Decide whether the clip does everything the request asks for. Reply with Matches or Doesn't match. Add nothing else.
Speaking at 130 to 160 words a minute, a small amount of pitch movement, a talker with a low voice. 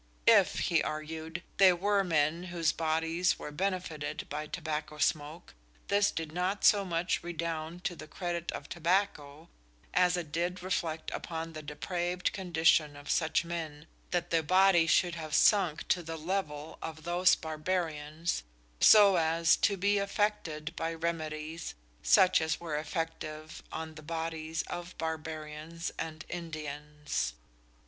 Doesn't match